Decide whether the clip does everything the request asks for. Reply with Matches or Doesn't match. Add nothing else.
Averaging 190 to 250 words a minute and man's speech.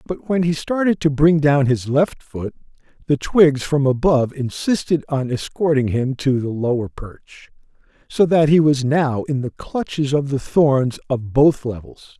Doesn't match